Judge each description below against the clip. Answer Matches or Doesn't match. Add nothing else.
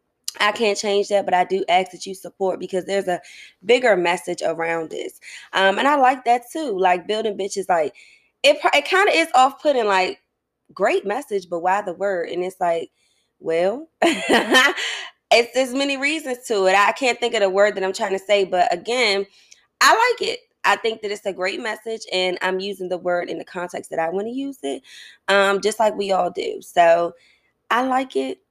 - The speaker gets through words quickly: Matches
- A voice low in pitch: Doesn't match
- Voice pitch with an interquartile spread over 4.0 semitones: Matches